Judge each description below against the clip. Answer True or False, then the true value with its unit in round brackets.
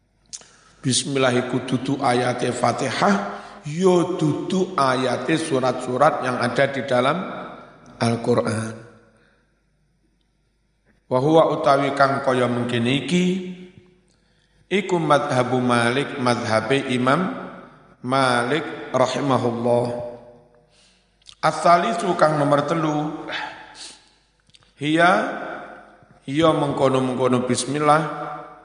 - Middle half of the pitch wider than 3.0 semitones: True (3.8 semitones)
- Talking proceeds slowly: True (75 wpm)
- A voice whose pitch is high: False (135 Hz)